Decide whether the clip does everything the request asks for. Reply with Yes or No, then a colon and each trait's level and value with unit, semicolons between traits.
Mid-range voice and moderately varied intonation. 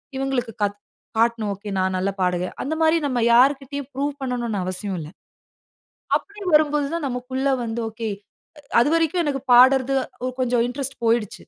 No: very high, 250 Hz; average, 3.8 semitones